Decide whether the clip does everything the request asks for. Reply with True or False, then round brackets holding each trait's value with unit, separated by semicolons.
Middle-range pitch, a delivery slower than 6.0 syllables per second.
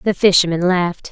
False (180 Hz; 6.1 syllables/s)